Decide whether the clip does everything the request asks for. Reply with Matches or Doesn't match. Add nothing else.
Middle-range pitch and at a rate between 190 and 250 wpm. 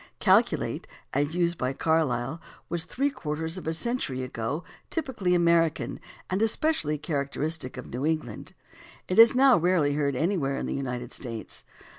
Doesn't match